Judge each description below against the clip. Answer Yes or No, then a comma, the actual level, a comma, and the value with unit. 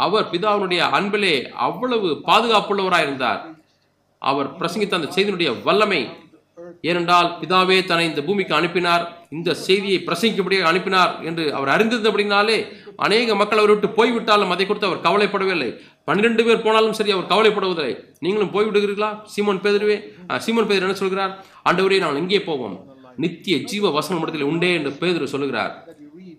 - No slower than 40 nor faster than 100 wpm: No, average, 125 wpm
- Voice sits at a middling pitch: No, high, 195 Hz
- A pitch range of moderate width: Yes, average, 3.4 semitones